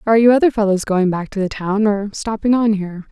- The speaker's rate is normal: No, fast, 250 wpm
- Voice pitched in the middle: No, high, 205 Hz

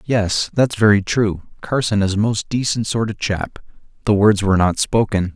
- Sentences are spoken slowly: No, average, 190 wpm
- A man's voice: Yes, male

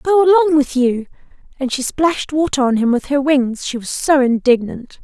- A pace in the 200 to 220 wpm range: Yes, fast, 205 wpm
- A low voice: No, very high, 275 Hz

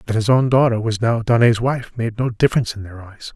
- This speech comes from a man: Yes, male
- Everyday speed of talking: No, fast, 250 wpm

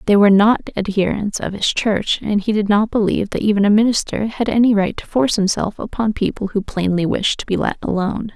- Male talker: No, female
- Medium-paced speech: No, fast, 225 wpm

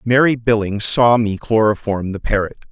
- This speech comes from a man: Yes, male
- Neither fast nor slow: Yes, average, 155 wpm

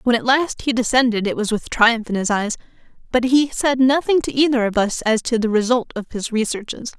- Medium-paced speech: No, fast, 230 wpm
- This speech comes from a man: No, female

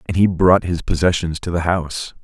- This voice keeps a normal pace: No, fast, 215 wpm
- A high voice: No, very low, 85 Hz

